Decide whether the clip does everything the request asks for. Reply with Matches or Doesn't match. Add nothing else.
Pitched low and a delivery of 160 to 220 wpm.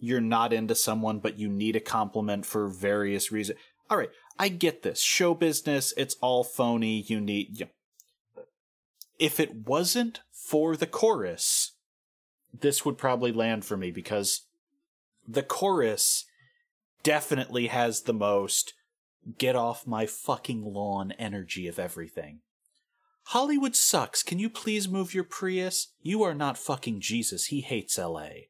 Doesn't match